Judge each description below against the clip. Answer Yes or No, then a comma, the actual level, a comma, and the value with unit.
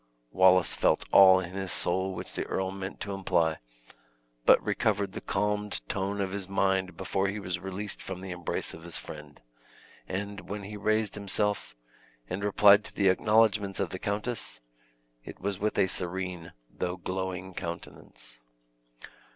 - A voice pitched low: Yes, very low, 95 Hz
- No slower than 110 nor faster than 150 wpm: No, average, 160 wpm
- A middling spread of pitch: No, narrow, 1.7 semitones